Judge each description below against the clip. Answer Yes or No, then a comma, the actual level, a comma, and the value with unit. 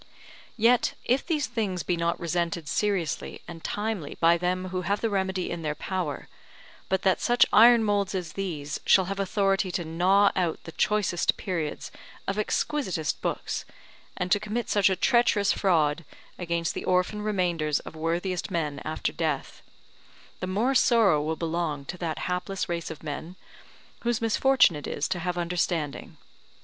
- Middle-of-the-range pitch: Yes, medium, 180 Hz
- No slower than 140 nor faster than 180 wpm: Yes, average, 160 wpm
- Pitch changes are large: No, average, 3.5 semitones